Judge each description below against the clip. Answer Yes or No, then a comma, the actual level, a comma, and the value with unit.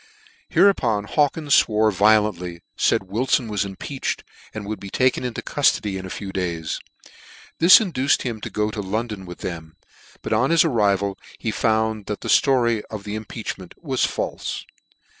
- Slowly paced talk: No, average, 165 wpm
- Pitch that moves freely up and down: No, average, 4.1 semitones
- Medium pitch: No, low, 110 Hz